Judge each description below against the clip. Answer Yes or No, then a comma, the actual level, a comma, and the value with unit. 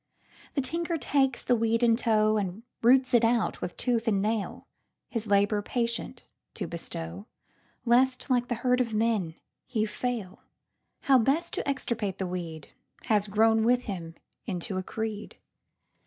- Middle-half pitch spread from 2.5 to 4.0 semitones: Yes, average, 3.4 semitones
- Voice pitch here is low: No, high, 225 Hz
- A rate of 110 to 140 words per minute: Yes, slow, 135 wpm